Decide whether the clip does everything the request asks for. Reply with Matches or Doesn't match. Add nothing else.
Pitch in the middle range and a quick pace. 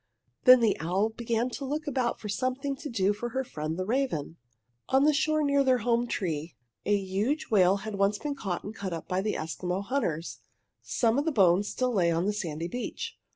Doesn't match